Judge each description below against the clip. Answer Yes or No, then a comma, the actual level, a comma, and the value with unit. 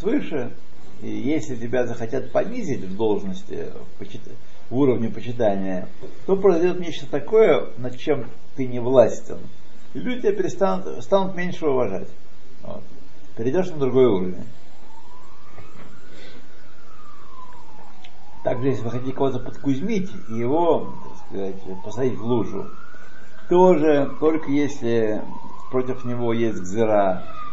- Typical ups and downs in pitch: No, wide, 7.3 semitones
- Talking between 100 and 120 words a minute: Yes, average, 115 wpm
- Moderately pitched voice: No, low, 130 Hz